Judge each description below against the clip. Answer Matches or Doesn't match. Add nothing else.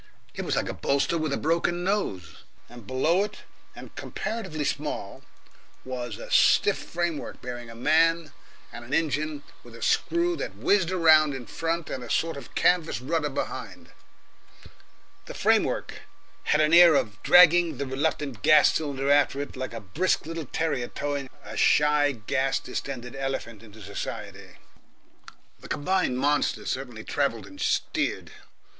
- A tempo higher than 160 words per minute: Doesn't match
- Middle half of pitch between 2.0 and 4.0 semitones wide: Doesn't match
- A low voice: Doesn't match